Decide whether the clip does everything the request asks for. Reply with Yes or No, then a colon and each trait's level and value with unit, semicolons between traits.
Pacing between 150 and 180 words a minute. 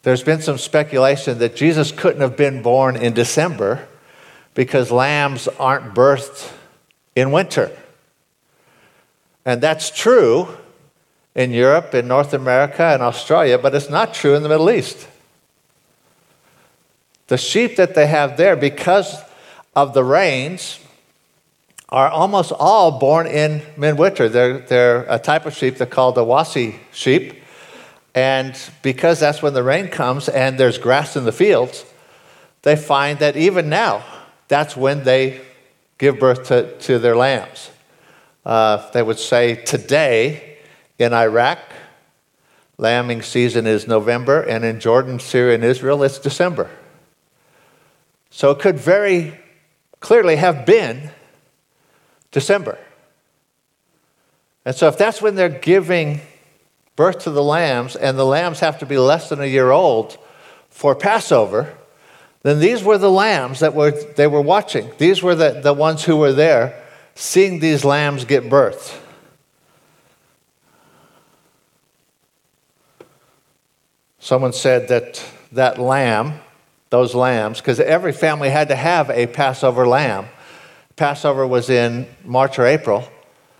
No: slow, 135 wpm